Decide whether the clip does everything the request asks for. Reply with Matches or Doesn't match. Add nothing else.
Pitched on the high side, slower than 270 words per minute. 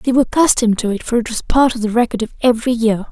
Doesn't match